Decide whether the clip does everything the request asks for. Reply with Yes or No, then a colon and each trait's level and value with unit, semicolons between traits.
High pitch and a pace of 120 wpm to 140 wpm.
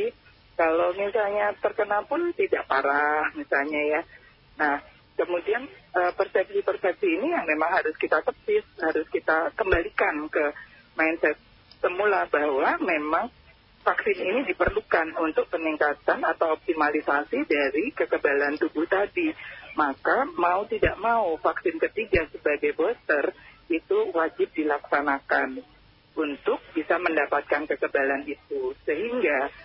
No: high, 230 Hz; average, 110 wpm